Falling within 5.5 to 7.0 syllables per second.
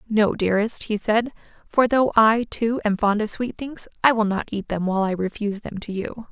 No: 5.2 syllables/s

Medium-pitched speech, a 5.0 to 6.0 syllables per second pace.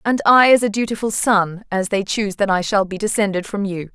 No: high, 205 Hz; 5.6 syllables/s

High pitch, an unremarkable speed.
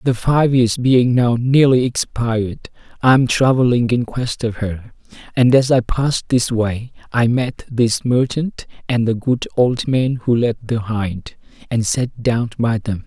No: low, 120 Hz; average, 175 wpm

